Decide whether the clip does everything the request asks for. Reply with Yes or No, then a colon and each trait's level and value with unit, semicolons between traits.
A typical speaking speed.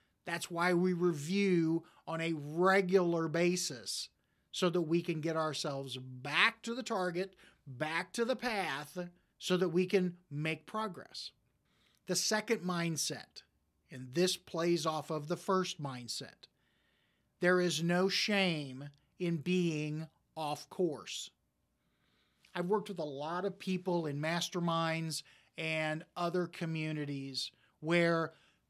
No: slow, 125 wpm